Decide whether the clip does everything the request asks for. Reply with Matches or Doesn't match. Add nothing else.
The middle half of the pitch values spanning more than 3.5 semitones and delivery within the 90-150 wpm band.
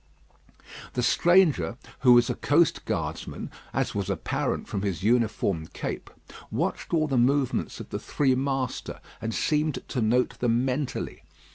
Matches